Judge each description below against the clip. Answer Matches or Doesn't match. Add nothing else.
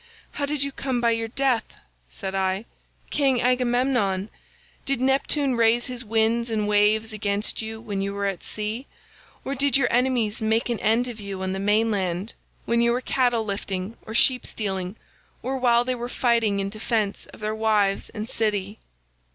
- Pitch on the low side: Doesn't match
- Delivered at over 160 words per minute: Matches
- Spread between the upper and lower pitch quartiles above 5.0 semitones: Doesn't match